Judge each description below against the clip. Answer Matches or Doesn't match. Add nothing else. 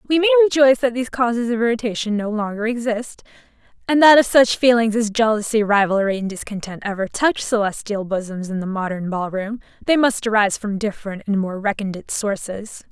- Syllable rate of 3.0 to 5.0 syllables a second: Doesn't match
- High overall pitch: Matches